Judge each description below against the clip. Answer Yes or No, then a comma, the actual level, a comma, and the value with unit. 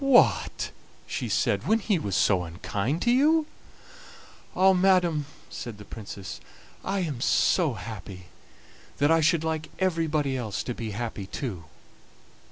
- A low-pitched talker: No, medium, 145 Hz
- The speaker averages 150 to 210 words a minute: No, average, 140 wpm